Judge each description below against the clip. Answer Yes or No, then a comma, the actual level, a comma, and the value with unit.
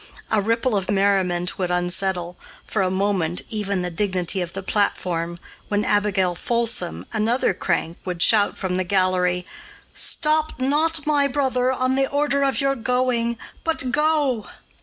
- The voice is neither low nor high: No, high, 205 Hz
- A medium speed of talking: Yes, average, 150 wpm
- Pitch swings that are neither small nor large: No, wide, 6.0 semitones